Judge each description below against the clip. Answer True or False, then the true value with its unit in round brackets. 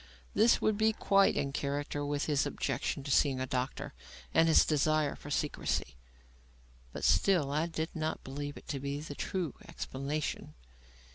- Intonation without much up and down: True (2.3 semitones)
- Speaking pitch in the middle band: True (145 Hz)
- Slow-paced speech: False (160 wpm)